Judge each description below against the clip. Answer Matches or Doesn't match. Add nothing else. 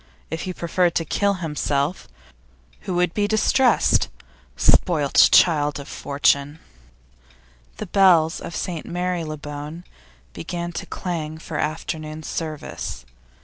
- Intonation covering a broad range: Doesn't match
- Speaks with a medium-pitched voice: Matches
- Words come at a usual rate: Doesn't match